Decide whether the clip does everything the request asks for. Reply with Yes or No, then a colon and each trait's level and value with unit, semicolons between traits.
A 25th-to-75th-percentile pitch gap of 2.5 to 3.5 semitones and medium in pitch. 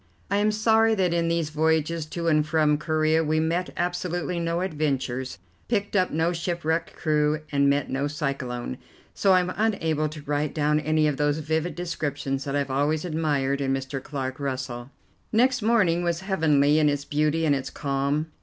Yes: average, 3.1 semitones; medium, 155 Hz